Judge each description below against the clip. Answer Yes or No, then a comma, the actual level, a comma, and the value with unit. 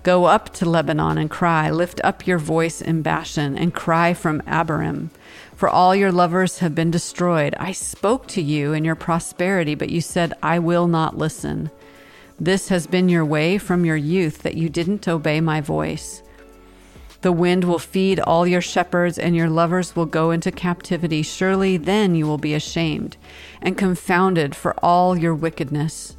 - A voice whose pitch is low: No, medium, 170 Hz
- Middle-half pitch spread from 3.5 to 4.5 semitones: No, narrow, 2.4 semitones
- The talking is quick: No, average, 175 wpm